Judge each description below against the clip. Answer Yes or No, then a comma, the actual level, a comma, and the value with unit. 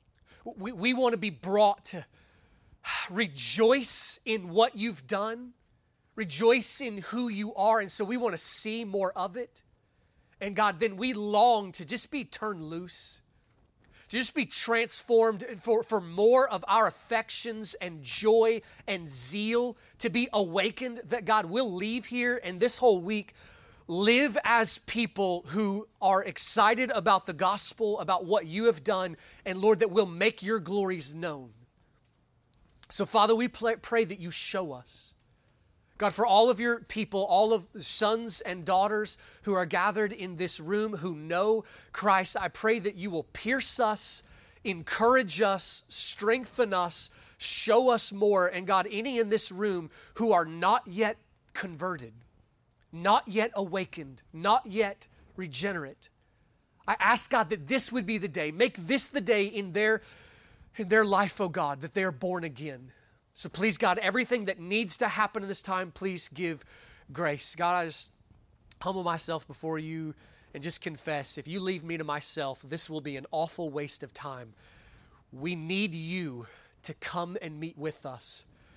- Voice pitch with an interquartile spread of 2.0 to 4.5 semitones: No, average, 4.9 semitones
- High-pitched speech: Yes, high, 200 Hz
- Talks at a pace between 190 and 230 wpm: No, average, 165 wpm